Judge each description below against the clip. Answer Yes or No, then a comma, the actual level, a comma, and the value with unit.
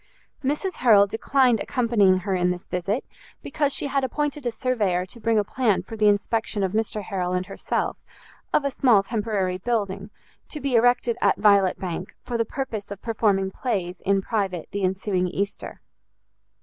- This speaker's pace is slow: No, average, 175 wpm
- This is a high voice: Yes, high, 210 Hz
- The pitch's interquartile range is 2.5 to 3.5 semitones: No, average, 4.0 semitones